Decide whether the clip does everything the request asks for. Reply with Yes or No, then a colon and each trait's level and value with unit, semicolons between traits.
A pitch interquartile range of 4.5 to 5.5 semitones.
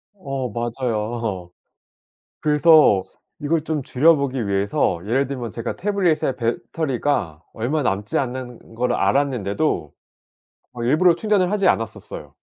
Yes: average, 5.2 semitones